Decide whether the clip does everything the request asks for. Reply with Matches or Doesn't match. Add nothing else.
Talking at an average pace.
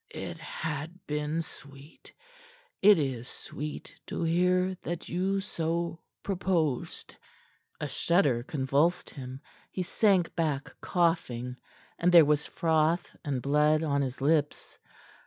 Doesn't match